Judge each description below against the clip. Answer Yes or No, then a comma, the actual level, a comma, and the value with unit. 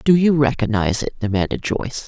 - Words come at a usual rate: Yes, average, 175 wpm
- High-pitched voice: No, low, 125 Hz